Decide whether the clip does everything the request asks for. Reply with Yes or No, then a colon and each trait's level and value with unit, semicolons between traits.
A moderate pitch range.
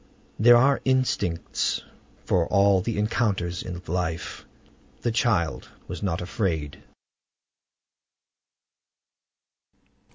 Yes: average, 5.0 semitones